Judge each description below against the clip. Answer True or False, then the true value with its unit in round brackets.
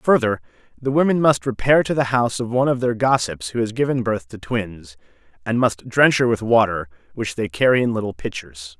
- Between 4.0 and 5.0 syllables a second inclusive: False (5.5 syllables/s)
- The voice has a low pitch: True (115 Hz)